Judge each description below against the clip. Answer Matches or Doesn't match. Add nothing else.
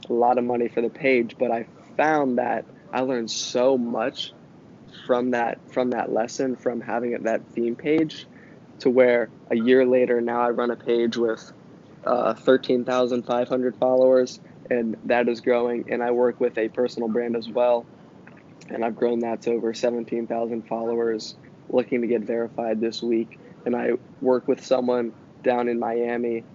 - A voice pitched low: Matches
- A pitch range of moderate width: Doesn't match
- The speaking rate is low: Doesn't match